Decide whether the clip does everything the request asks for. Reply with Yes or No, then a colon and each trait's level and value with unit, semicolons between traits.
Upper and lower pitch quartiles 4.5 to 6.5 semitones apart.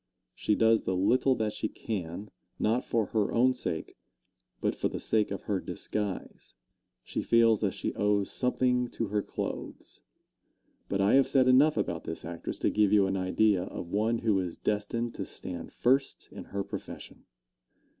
No: average, 3.2 semitones